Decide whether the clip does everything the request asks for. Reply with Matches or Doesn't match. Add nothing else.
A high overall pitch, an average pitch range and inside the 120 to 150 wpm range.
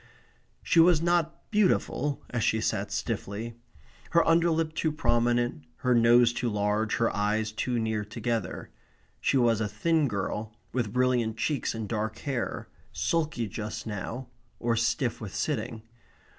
Doesn't match